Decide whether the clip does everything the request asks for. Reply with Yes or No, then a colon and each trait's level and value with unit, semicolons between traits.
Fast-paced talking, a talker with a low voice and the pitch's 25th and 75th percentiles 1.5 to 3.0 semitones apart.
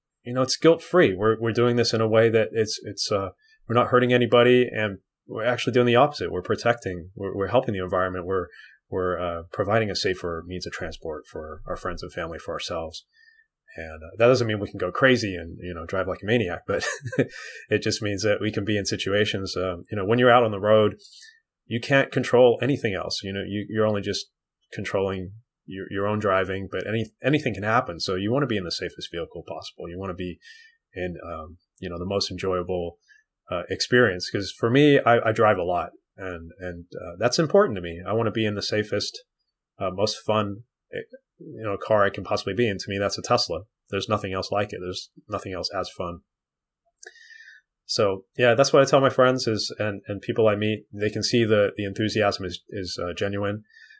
No: fast, 220 wpm; low, 105 Hz; average, 4.2 semitones